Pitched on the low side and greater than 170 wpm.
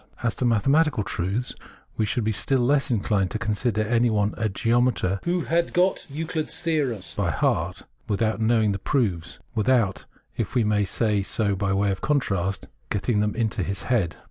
Yes: low, 110 Hz; average, 195 wpm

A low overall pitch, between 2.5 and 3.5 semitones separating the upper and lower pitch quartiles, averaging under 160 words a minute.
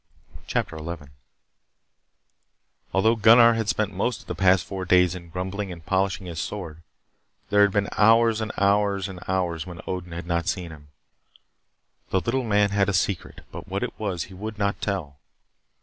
No: very low, 95 Hz; average, 3.0 semitones; average, 165 wpm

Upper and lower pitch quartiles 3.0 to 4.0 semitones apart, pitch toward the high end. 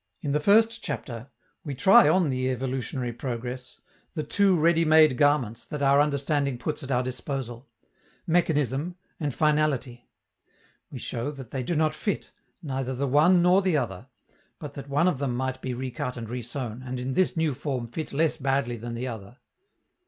No: average, 3.6 semitones; low, 135 Hz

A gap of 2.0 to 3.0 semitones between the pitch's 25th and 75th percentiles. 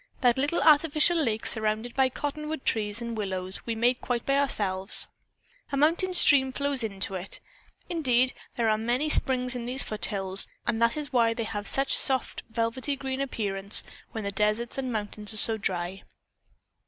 No: average, 4.2 semitones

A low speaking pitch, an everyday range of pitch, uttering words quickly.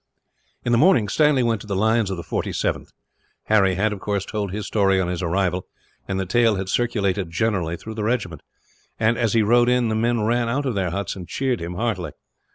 Yes: low, 105 Hz; average, 3.7 semitones; fast, 220 wpm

